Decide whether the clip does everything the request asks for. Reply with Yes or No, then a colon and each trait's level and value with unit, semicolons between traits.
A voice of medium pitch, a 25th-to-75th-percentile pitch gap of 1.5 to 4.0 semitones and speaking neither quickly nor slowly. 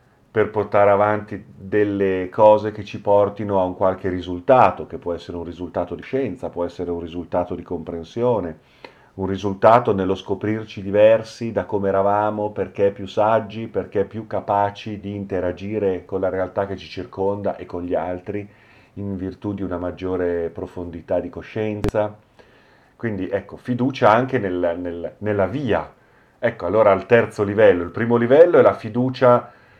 No: low, 100 Hz; average, 2.8 semitones; average, 155 wpm